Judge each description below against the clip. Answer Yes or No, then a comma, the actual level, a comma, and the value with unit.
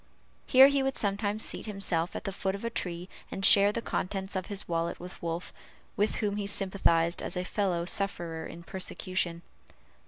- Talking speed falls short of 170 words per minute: No, average, 185 wpm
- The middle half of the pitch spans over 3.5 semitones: No, average, 3.0 semitones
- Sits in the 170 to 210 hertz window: Yes, high, 190 Hz